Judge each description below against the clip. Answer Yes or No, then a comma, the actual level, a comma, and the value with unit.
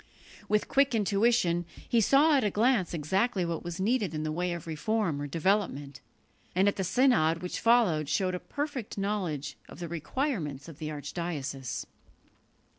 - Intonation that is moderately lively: No, wide, 6.1 semitones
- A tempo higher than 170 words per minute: No, average, 165 wpm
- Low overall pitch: No, medium, 180 Hz